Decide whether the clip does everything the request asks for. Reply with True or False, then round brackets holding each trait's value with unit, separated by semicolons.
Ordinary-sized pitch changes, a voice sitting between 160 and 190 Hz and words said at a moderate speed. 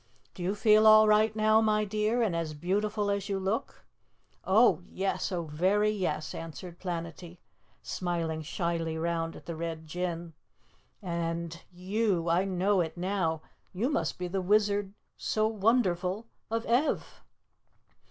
True (3.9 semitones; 185 Hz; 145 wpm)